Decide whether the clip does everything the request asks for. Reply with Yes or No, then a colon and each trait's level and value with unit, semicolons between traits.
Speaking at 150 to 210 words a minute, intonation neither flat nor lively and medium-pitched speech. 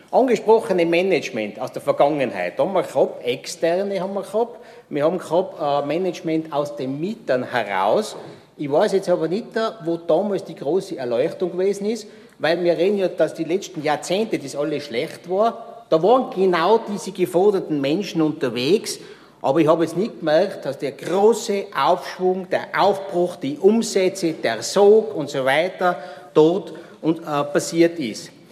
Yes: average, 160 wpm; average, 4.0 semitones; medium, 180 Hz